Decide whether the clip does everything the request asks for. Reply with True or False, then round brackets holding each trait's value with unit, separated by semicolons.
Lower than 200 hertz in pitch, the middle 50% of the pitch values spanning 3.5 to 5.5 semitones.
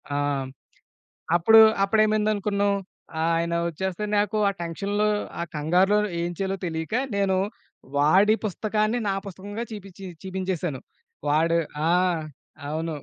True (190 Hz; 3.8 semitones)